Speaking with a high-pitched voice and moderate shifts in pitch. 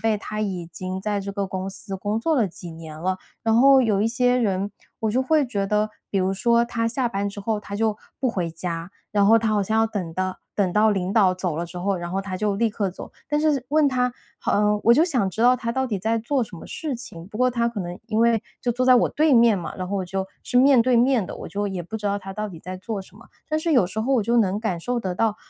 Yes: high, 210 Hz; average, 3.8 semitones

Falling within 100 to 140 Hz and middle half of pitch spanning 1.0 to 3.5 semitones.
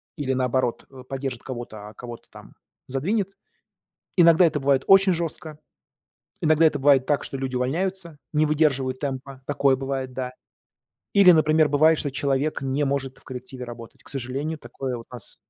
Yes: low, 135 Hz; average, 3.1 semitones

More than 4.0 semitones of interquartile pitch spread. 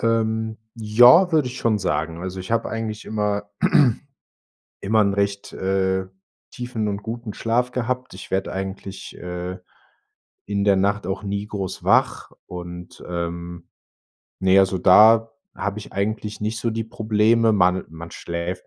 No: average, 3.1 semitones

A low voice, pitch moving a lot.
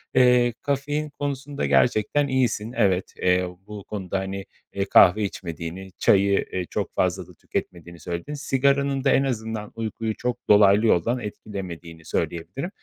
Yes: low, 105 Hz; wide, 5.8 semitones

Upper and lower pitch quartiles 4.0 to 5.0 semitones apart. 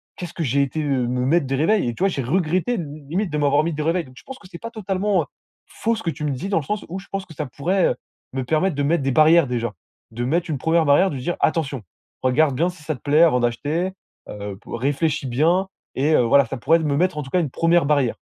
Yes: average, 4.5 semitones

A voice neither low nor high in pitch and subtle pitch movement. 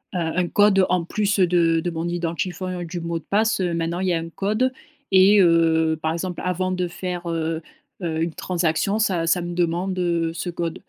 Yes: medium, 175 Hz; narrow, 1.9 semitones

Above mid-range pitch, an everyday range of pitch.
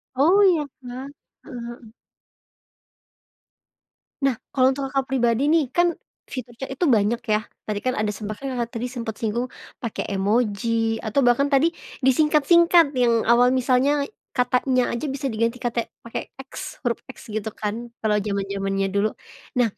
Yes: high, 245 Hz; average, 3.4 semitones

